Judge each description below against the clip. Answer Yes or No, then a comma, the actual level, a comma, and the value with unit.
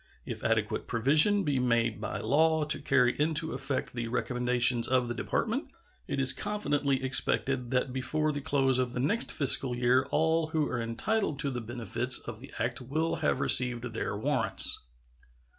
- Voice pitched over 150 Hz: No, low, 130 Hz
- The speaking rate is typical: Yes, average, 170 wpm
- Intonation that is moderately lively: Yes, average, 3.4 semitones